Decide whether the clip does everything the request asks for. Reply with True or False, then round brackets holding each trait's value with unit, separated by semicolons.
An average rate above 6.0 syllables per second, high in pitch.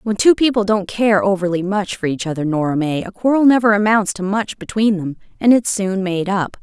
False (5.4 syllables/s; 200 Hz)